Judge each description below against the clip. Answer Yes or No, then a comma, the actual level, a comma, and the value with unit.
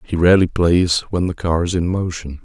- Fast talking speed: Yes, fast, 220 wpm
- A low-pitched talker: Yes, very low, 85 Hz